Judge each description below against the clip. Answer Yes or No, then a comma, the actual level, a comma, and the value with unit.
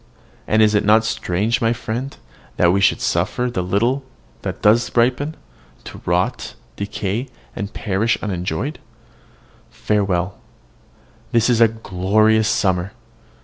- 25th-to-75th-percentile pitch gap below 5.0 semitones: Yes, average, 3.3 semitones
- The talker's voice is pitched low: Yes, low, 110 Hz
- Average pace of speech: No, slow, 130 wpm